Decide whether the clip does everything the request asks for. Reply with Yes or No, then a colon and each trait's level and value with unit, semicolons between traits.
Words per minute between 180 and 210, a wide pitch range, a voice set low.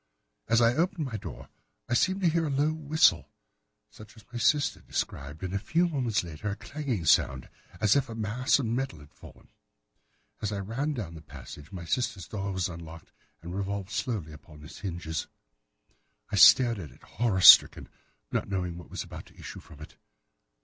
Yes: average, 190 wpm; wide, 7.2 semitones; low, 105 Hz